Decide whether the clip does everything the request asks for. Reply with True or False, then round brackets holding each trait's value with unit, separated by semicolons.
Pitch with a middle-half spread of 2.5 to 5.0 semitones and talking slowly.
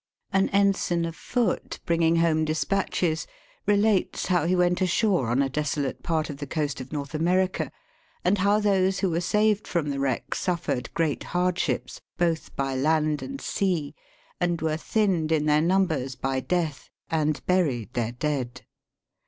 False (3.9 semitones; 160 wpm)